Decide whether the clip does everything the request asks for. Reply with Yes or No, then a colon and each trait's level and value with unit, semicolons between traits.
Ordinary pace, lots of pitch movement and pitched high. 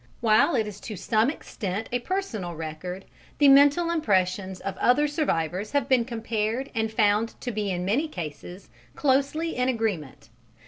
Yes: average, 155 wpm; wide, 6.1 semitones; high, 220 Hz